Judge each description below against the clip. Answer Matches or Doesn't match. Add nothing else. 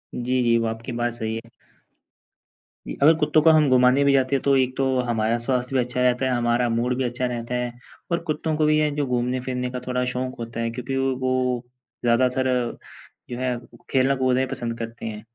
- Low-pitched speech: Matches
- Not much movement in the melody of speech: Matches